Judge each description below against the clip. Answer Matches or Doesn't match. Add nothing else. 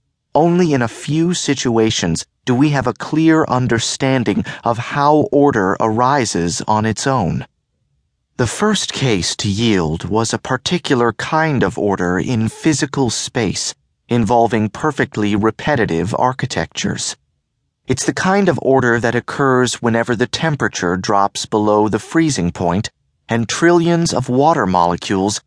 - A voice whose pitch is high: Doesn't match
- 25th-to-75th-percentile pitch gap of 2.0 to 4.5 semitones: Doesn't match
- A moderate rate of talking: Doesn't match